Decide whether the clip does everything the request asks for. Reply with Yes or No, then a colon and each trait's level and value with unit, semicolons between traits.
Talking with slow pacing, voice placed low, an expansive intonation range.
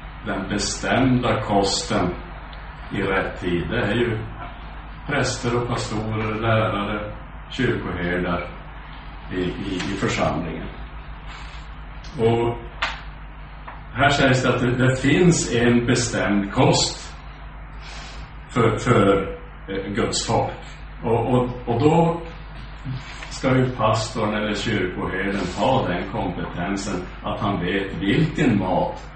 No: slow, 105 wpm; low, 110 Hz; average, 4.2 semitones